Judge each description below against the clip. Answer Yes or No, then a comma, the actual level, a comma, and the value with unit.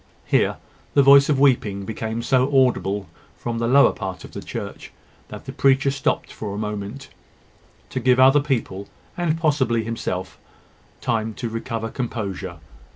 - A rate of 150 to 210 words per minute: Yes, average, 155 wpm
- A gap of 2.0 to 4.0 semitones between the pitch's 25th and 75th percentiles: No, average, 4.5 semitones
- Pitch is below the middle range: Yes, low, 115 Hz